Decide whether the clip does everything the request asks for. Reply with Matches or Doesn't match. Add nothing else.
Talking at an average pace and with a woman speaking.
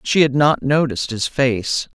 Doesn't match